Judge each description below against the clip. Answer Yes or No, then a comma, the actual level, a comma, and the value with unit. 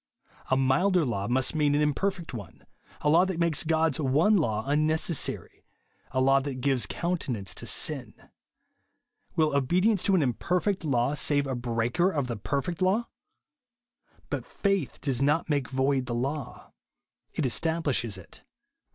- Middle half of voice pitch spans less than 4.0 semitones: No, average, 4.6 semitones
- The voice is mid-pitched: Yes, medium, 145 Hz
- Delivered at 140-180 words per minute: Yes, average, 160 wpm